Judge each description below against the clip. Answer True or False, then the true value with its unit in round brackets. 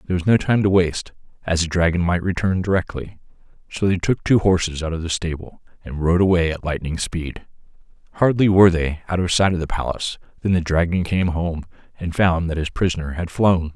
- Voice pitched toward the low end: True (85 Hz)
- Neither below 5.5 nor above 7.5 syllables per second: True (5.8 syllables/s)